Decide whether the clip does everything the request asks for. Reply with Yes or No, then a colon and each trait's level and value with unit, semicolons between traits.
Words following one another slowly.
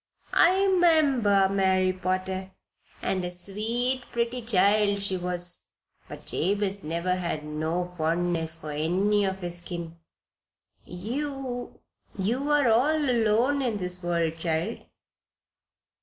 Yes: slow, 115 wpm